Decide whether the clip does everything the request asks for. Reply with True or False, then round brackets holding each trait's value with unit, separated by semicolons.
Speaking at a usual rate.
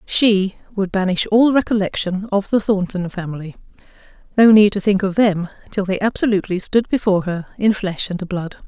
True (165 wpm)